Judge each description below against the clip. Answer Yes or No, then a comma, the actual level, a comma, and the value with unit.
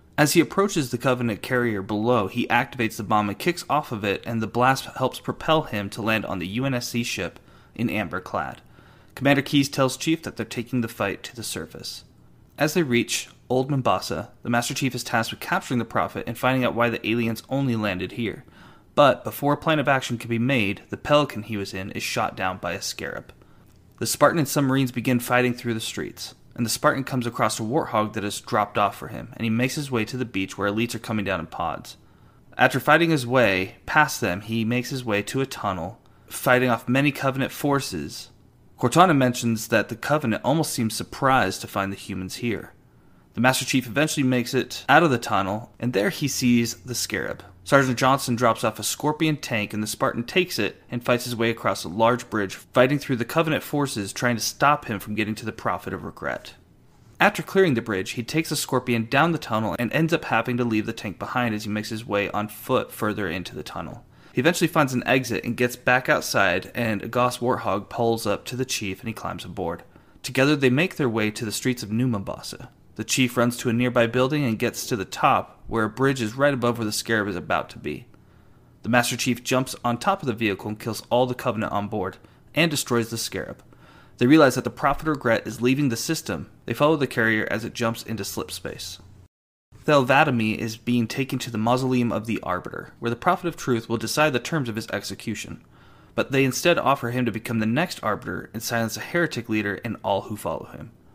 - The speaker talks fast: Yes, fast, 225 wpm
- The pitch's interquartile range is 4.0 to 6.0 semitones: No, average, 3.4 semitones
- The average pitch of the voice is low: Yes, low, 120 Hz